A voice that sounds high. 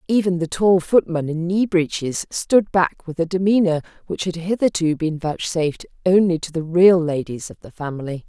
No: medium, 175 Hz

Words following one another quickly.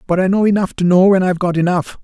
Yes: fast, 295 wpm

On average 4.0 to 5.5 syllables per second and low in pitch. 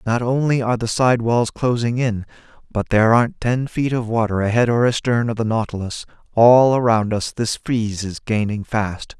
Yes: 5.1 syllables/s; low, 115 Hz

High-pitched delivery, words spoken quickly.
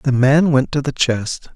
No: low, 135 Hz; fast, 230 wpm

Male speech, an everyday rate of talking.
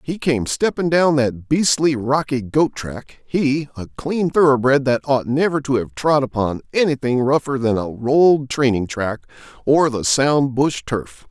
Yes: male; average, 170 wpm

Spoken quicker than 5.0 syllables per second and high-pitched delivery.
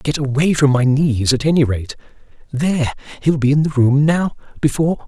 No: 5.4 syllables/s; medium, 140 Hz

